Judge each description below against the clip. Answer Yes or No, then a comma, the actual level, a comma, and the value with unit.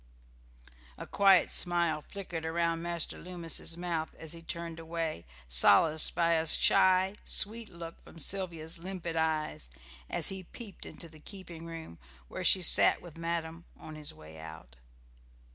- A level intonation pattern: Yes, narrow, 1.6 semitones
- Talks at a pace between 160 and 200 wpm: No, average, 145 wpm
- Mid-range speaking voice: Yes, medium, 165 Hz